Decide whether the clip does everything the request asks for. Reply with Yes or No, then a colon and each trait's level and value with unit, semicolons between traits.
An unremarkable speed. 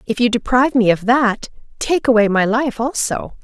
Yes: average, 190 wpm